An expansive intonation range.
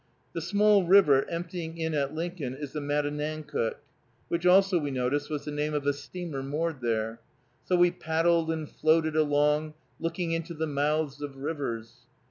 No: narrow, 2.6 semitones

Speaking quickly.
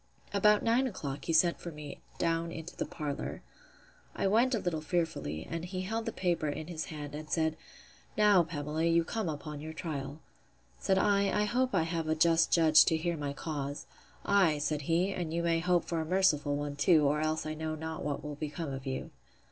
Yes: fast, 210 wpm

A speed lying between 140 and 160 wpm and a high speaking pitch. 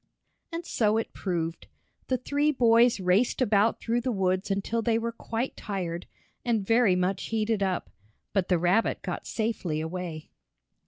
Yes: average, 155 wpm; high, 210 Hz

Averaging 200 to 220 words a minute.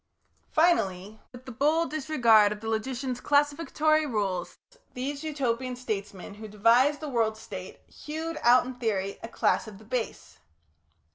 No: average, 145 wpm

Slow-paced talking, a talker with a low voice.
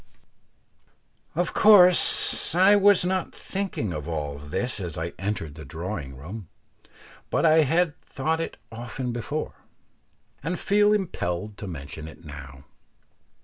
Yes: slow, 130 wpm; low, 110 Hz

